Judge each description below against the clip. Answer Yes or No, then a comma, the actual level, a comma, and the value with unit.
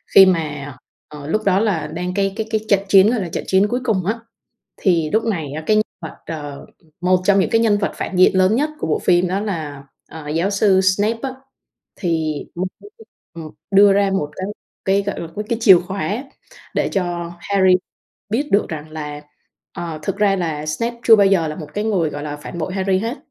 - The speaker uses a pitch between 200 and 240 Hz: No, high, 190 Hz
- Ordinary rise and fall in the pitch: Yes, average, 4.3 semitones